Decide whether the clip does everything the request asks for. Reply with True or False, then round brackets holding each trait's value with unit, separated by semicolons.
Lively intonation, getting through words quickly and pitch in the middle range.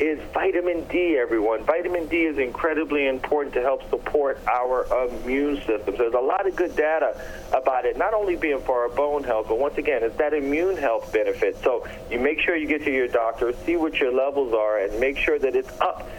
True (5.8 semitones; 220 wpm; 150 Hz)